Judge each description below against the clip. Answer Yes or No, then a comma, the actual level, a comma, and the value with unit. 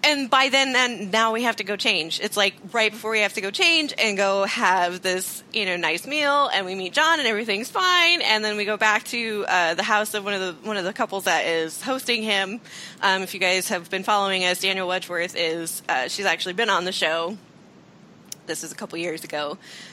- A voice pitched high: Yes, high, 205 Hz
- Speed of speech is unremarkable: No, fast, 245 wpm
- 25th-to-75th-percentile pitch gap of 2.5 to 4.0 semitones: Yes, average, 3.4 semitones